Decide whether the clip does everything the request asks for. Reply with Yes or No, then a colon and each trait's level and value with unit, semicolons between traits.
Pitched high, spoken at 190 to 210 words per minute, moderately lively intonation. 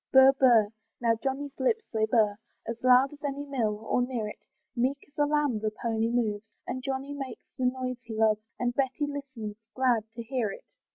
Yes: very high, 250 Hz; average, 195 wpm; average, 3.4 semitones